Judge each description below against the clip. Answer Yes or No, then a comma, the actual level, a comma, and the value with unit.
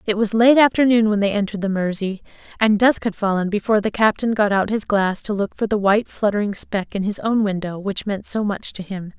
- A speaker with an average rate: No, fast, 240 wpm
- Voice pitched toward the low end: No, high, 205 Hz